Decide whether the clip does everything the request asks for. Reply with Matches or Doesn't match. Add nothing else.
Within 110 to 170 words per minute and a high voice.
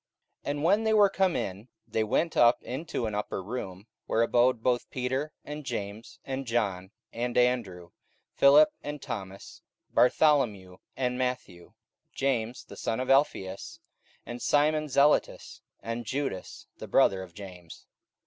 Doesn't match